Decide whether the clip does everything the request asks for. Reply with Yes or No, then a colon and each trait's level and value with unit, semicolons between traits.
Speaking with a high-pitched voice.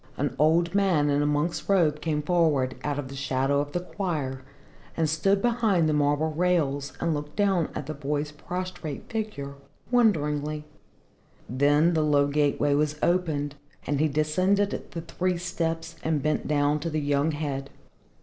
No: medium, 150 Hz